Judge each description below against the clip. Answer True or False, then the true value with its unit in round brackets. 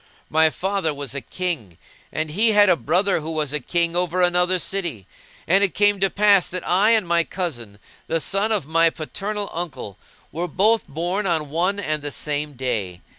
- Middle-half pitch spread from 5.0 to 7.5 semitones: False (4.4 semitones)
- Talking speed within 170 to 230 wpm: True (190 wpm)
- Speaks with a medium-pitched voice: True (170 Hz)